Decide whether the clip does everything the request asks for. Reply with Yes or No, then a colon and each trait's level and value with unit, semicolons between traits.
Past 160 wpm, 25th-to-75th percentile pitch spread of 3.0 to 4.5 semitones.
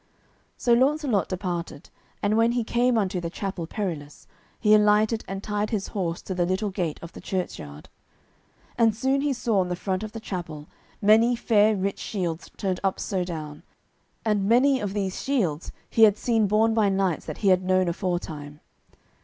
Yes: average, 180 wpm; average, 3.7 semitones